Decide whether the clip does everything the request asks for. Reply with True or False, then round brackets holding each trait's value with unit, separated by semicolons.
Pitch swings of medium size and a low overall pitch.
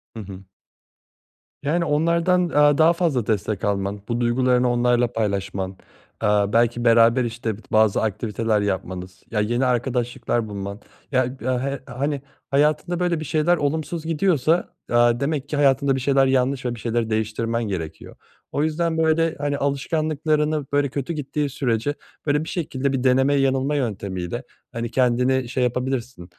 True (4.3 semitones; 130 Hz)